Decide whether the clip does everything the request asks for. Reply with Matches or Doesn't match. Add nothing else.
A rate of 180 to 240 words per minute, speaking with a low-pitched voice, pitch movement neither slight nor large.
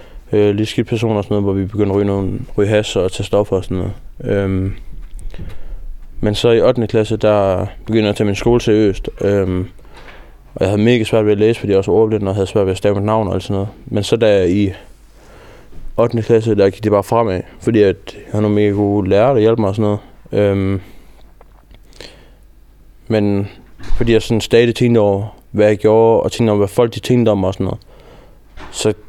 Doesn't match